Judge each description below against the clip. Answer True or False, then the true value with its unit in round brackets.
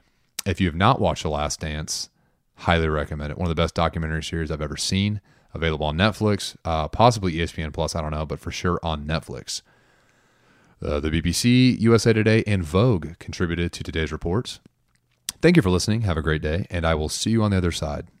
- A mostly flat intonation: False (4.2 semitones)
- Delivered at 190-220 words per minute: True (205 wpm)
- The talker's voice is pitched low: True (85 Hz)